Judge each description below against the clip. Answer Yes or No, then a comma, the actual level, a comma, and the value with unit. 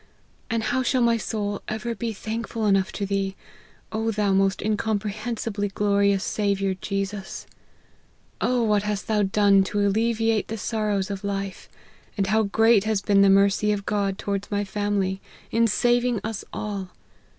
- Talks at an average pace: Yes, average, 160 wpm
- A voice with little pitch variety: Yes, narrow, 2.0 semitones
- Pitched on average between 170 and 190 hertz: No, high, 205 Hz